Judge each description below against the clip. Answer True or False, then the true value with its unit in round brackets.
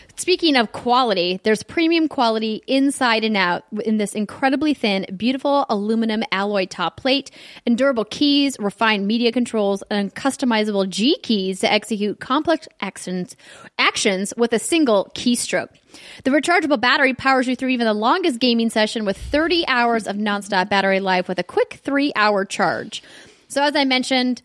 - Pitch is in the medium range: False (230 Hz)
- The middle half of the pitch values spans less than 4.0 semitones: False (4.9 semitones)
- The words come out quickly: False (155 wpm)